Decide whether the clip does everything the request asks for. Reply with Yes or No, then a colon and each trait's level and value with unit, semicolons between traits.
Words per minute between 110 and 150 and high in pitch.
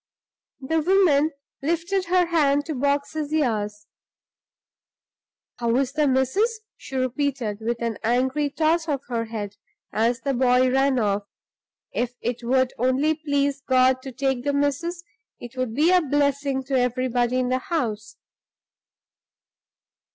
Yes: average, 140 wpm; very high, 265 Hz